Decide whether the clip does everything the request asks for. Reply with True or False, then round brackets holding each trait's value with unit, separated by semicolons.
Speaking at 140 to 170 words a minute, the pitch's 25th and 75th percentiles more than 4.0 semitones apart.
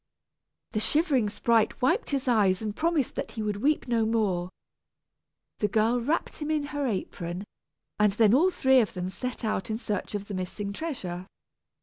False (180 wpm; 4.9 semitones)